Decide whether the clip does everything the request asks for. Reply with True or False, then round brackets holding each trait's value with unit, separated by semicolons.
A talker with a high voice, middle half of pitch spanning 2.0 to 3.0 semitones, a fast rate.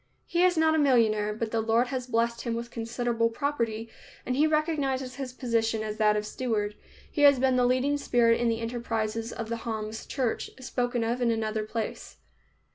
False (235 Hz; 2.4 semitones; 195 wpm)